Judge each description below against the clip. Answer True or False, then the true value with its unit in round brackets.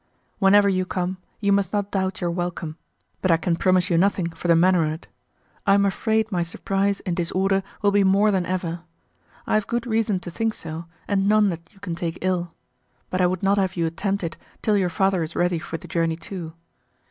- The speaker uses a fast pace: True (220 wpm)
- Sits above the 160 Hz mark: True (185 Hz)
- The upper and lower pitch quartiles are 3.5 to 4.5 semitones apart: False (2.7 semitones)